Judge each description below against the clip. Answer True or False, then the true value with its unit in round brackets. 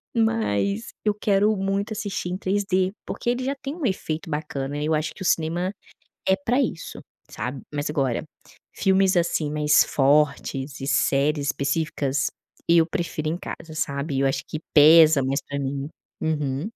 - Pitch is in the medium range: True (160 Hz)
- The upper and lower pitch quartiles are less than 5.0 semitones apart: False (5.4 semitones)